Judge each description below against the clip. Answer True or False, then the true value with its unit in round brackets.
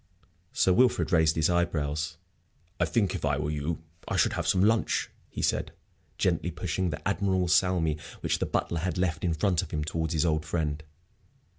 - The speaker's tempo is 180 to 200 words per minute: True (185 wpm)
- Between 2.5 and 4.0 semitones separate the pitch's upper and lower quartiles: True (2.9 semitones)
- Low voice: True (85 Hz)